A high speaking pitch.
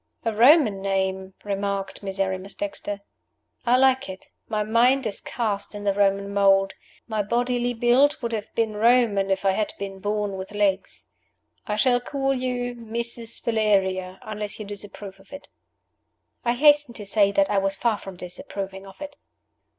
Yes: high, 210 Hz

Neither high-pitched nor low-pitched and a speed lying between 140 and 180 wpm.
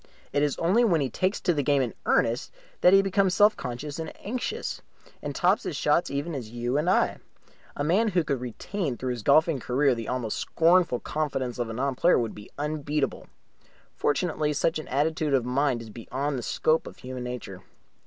No: medium, 145 Hz; average, 200 wpm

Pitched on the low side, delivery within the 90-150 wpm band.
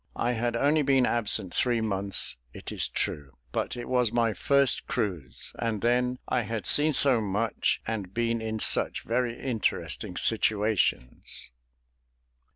Yes: low, 115 Hz; average, 145 wpm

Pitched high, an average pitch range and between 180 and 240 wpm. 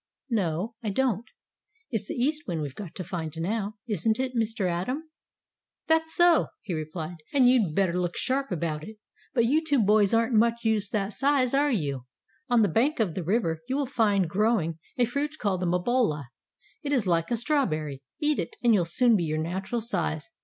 No: high, 215 Hz; wide, 6.4 semitones; average, 195 wpm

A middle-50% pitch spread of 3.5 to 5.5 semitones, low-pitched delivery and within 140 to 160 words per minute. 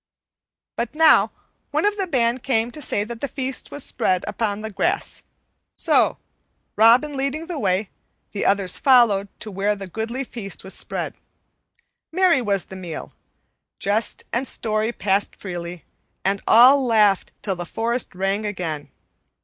No: average, 4.7 semitones; high, 220 Hz; average, 150 wpm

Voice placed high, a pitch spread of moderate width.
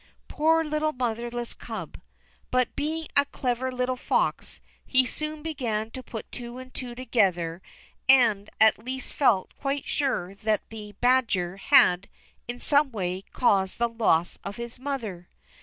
Yes: high, 240 Hz; average, 4.0 semitones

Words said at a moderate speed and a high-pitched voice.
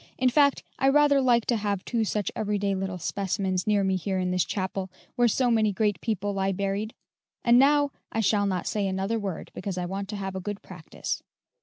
No: fast, 215 wpm; high, 200 Hz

